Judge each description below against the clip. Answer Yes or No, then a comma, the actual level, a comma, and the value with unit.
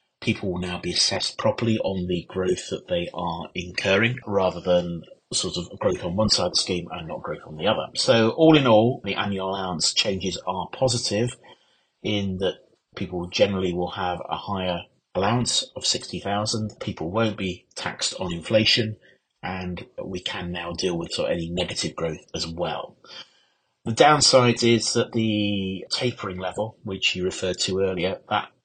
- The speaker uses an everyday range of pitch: Yes, average, 3.8 semitones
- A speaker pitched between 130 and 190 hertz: No, very low, 95 Hz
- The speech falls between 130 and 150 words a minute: No, average, 175 wpm